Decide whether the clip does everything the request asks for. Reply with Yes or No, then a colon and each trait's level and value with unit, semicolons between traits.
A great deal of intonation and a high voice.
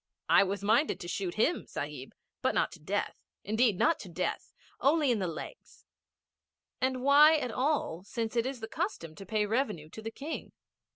Yes: wide, 6.4 semitones; high, 225 Hz